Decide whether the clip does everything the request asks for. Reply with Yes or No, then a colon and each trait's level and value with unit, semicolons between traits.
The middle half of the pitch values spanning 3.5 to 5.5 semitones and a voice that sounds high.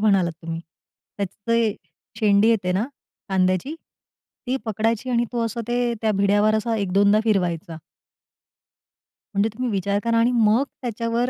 No: average, 2.7 semitones; high, 215 Hz